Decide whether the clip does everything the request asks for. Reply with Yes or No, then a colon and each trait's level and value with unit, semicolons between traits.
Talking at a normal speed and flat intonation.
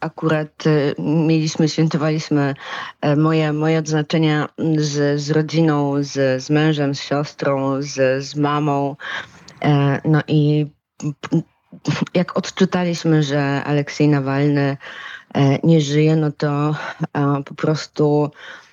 No: slow, 95 wpm; narrow, 1.7 semitones